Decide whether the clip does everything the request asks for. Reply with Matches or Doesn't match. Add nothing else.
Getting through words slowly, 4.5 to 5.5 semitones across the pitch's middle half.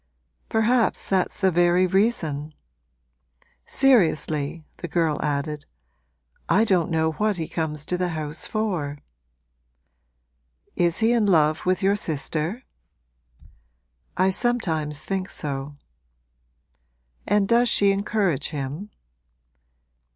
Matches